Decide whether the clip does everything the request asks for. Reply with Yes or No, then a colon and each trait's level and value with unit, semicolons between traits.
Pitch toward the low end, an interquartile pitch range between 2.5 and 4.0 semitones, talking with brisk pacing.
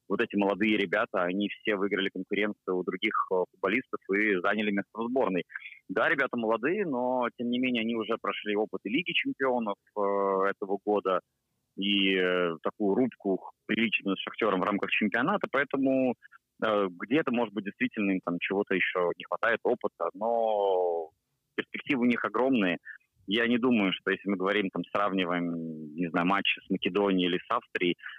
Yes: low, 100 Hz; average, 2.9 semitones; fast, 165 wpm